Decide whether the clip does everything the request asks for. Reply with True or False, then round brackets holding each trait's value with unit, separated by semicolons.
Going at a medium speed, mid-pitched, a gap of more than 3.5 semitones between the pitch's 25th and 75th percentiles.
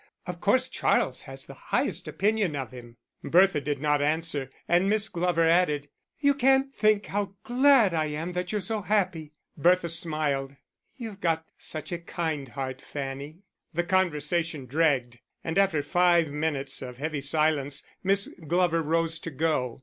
True (155 wpm; 165 Hz; 4.2 semitones)